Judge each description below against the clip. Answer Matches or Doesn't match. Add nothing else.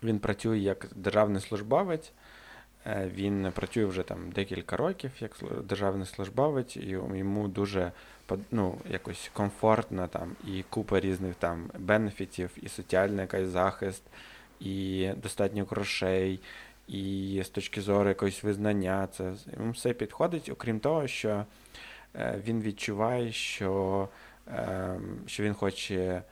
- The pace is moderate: Matches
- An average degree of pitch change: Doesn't match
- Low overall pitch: Matches